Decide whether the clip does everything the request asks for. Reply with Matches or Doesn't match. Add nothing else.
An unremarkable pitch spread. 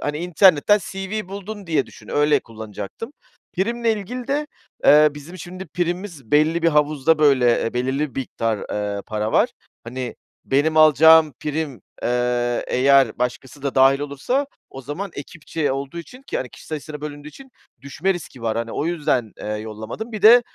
Doesn't match